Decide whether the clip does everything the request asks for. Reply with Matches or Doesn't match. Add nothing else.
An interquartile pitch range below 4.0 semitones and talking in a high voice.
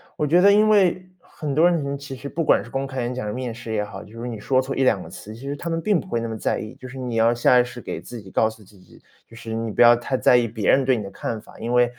Doesn't match